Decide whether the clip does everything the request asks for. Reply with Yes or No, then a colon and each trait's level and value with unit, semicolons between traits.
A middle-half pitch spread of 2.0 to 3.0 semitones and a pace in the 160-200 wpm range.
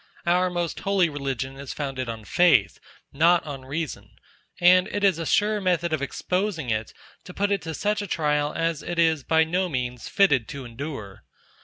No: average, 4.8 semitones; average, 185 wpm